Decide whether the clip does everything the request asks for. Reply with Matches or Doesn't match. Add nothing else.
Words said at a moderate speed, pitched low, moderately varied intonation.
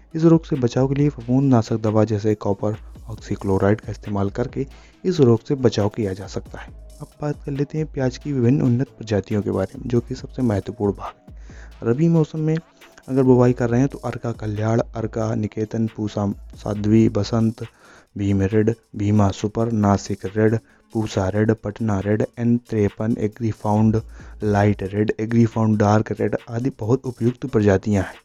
Matches